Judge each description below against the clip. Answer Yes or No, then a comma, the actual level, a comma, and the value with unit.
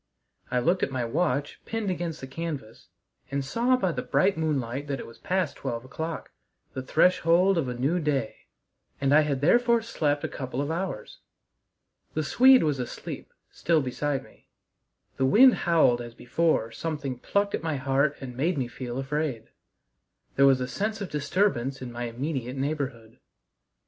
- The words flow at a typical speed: Yes, average, 170 wpm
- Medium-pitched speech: Yes, medium, 145 Hz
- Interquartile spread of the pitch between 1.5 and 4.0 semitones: No, average, 4.7 semitones